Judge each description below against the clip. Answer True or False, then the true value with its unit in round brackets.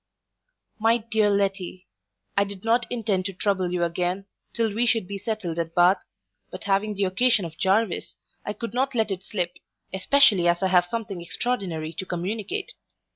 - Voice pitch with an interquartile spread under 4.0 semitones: True (3.6 semitones)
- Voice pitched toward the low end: False (195 Hz)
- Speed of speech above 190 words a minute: False (175 wpm)